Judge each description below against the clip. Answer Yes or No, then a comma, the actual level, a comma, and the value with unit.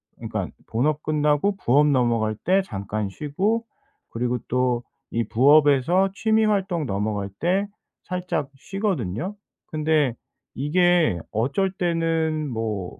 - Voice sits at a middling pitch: Yes, medium, 150 Hz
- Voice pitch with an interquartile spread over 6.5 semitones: Yes, wide, 7.2 semitones